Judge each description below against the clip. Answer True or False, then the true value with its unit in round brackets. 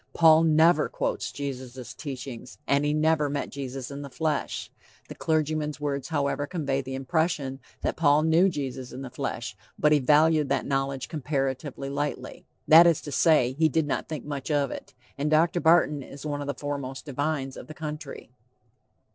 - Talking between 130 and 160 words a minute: False (180 wpm)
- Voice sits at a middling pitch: True (145 Hz)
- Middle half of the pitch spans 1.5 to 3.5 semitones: True (2.4 semitones)